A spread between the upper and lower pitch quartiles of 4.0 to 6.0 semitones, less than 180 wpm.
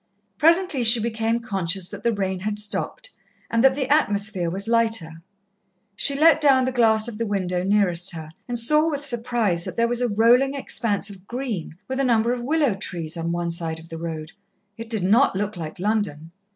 No: average, 5.1 semitones; average, 200 wpm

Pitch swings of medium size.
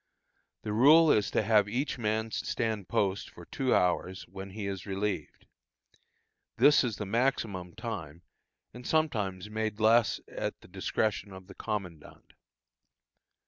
Yes: average, 3.1 semitones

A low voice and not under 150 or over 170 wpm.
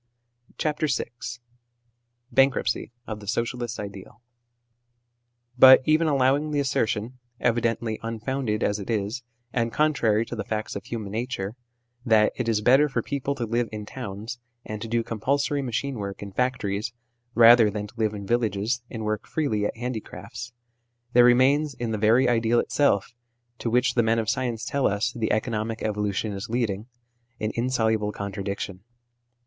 Yes: low, 115 Hz; average, 155 wpm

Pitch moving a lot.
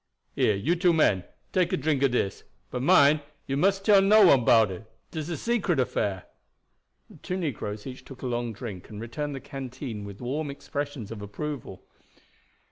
Yes: wide, 5.8 semitones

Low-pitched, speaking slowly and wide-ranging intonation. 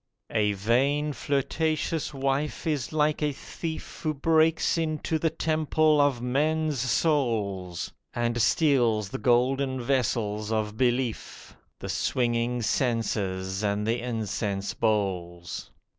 Yes: low, 125 Hz; slow, 115 wpm; wide, 5.7 semitones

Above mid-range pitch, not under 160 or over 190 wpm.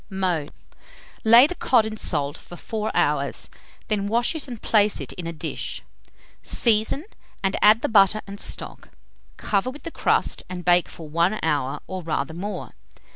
Yes: high, 200 Hz; average, 170 wpm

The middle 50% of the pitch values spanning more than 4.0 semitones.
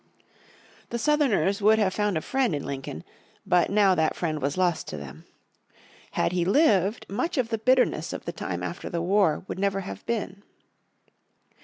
Yes: average, 4.5 semitones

